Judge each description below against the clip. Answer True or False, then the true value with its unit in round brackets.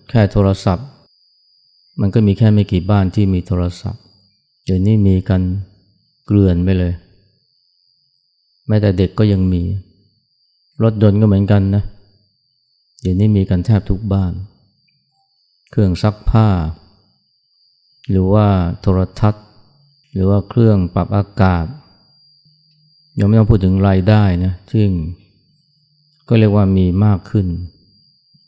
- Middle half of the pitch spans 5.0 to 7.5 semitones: True (5.4 semitones)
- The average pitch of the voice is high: False (105 Hz)